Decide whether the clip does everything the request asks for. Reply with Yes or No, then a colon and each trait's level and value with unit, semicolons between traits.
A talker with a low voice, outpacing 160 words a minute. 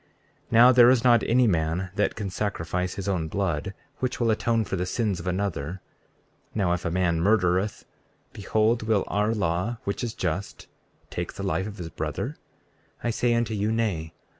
Yes: low, 100 Hz; average, 185 wpm